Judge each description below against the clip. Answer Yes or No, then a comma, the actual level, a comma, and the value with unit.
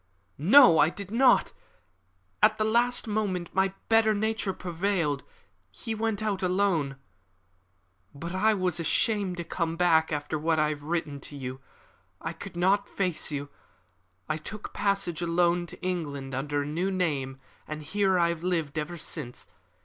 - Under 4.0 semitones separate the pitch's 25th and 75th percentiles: No, average, 4.7 semitones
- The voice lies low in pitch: No, medium, 175 Hz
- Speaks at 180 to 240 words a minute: No, average, 155 wpm